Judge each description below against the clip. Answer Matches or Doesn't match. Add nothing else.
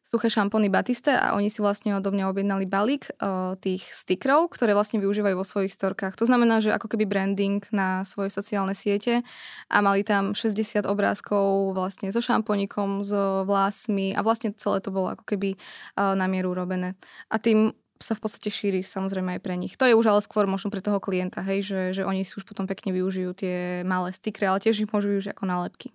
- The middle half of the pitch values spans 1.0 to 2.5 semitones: Matches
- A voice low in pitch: Doesn't match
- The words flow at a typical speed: Doesn't match